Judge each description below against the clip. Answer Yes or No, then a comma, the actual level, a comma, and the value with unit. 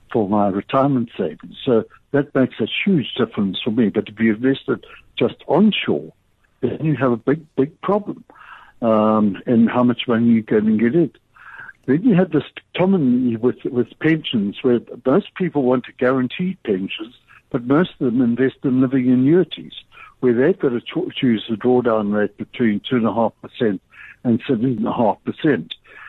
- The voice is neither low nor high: No, low, 125 Hz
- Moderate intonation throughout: Yes, average, 4.0 semitones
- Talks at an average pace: Yes, average, 160 wpm